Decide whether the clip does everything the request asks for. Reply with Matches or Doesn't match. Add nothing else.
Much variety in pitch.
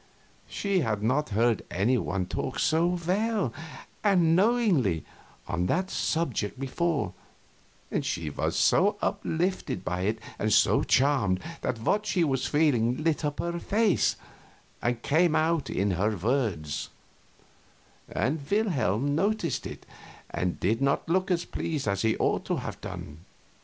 Matches